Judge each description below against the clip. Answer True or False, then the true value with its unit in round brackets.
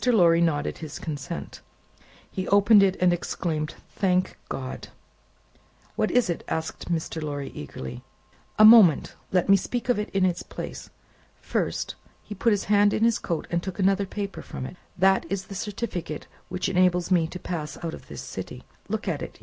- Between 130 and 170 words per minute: False (180 wpm)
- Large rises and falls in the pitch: False (3.5 semitones)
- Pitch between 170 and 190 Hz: True (185 Hz)